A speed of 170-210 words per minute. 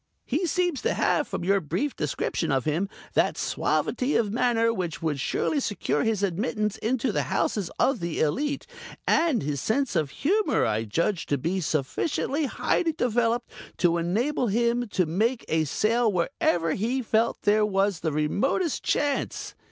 No: average, 160 wpm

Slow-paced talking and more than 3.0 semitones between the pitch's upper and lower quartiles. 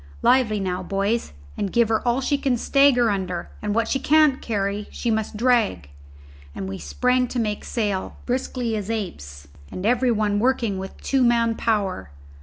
No: average, 175 wpm; average, 3.9 semitones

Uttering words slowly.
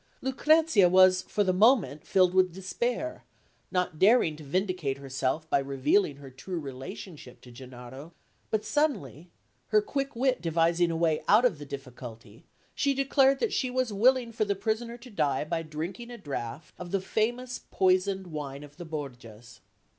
No: average, 165 wpm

